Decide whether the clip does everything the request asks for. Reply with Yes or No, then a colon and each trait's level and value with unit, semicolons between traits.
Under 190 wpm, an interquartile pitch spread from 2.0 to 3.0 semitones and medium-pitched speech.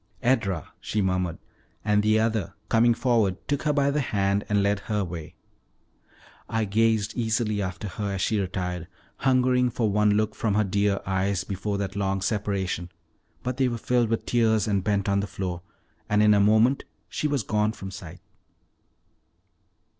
No: average, 170 wpm; narrow, 2.6 semitones; low, 105 Hz